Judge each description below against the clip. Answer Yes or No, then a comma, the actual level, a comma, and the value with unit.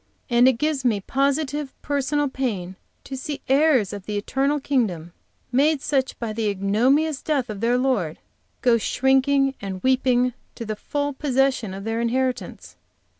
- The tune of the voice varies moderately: Yes, average, 4.3 semitones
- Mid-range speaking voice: No, very high, 255 Hz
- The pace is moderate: Yes, average, 155 wpm